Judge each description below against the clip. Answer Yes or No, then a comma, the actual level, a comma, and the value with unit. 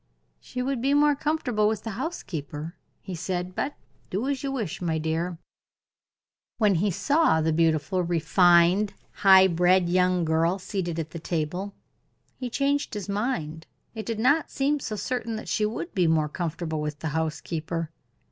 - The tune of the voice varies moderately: No, wide, 5.8 semitones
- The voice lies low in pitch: No, medium, 185 Hz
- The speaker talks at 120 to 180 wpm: Yes, average, 165 wpm